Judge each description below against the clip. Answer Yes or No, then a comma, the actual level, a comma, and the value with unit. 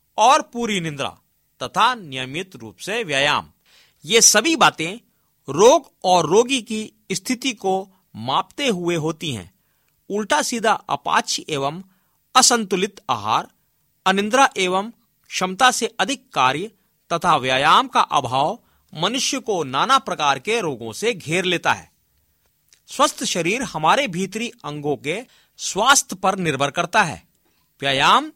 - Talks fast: No, average, 125 wpm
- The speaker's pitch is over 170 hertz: Yes, high, 190 Hz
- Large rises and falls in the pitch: Yes, wide, 7.3 semitones